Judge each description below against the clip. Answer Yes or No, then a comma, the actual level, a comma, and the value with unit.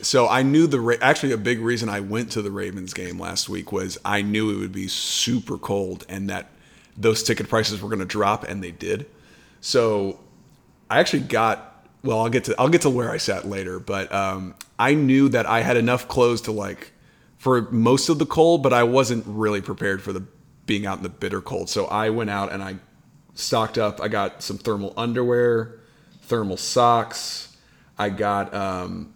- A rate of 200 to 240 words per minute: Yes, fast, 205 wpm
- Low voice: Yes, low, 110 Hz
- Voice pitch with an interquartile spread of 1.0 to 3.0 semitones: No, average, 3.5 semitones